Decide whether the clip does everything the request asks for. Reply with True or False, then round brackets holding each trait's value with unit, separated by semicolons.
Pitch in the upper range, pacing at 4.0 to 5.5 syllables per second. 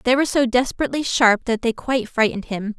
False (240 Hz; 6.7 syllables/s)